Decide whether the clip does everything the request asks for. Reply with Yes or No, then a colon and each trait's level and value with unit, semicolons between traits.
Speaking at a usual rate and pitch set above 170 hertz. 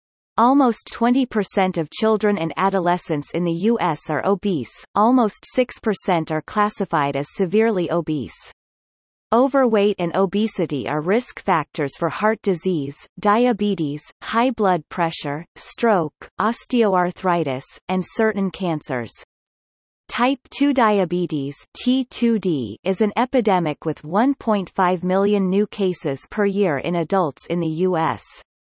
No: slow, 115 wpm; high, 190 Hz